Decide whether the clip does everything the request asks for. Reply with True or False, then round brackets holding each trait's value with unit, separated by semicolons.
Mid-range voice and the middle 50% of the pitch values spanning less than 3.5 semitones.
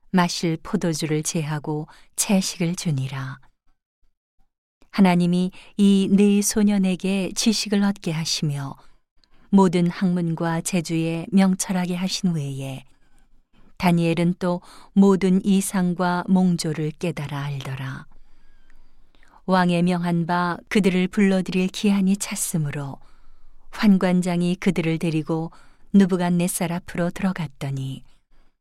True (180 Hz; 2.7 semitones)